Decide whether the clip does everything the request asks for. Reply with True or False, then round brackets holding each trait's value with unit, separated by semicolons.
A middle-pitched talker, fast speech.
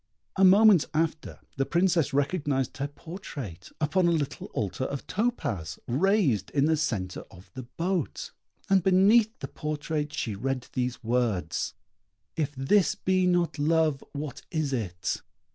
False (150 Hz; 145 wpm)